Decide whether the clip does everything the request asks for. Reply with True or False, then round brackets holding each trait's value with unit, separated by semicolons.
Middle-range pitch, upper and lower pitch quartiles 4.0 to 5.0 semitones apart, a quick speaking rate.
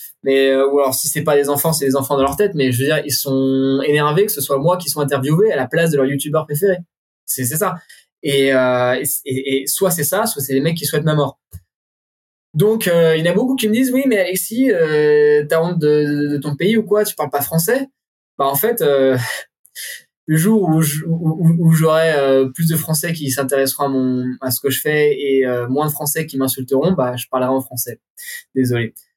True (150 Hz; 4.3 semitones; 235 wpm)